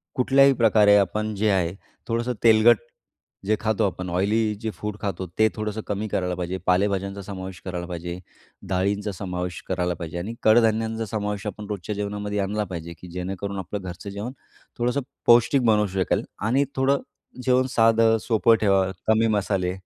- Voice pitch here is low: Yes, low, 105 Hz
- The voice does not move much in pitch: No, average, 3.1 semitones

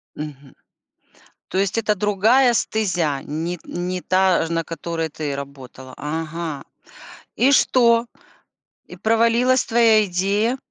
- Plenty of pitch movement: Yes, wide, 6.0 semitones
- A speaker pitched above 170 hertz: Yes, medium, 185 Hz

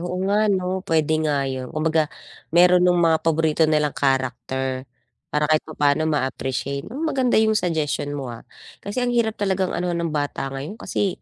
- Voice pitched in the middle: Yes, medium, 160 Hz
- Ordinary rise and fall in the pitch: Yes, average, 4.3 semitones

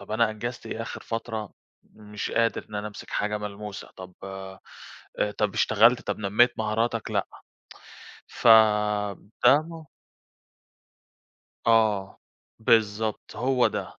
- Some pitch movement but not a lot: No, narrow, 1.9 semitones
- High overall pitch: No, low, 110 Hz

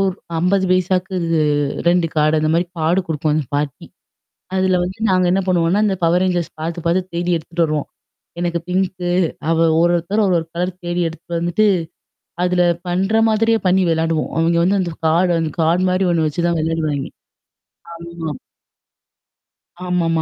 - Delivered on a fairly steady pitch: Yes, narrow, 2.0 semitones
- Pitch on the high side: No, medium, 175 Hz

